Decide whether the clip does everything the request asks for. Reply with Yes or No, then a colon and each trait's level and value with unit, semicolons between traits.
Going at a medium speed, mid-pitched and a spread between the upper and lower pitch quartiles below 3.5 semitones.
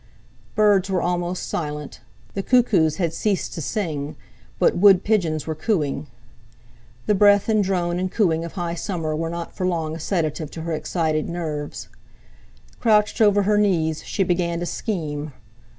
No: average, 160 wpm; medium, 175 Hz; average, 3.9 semitones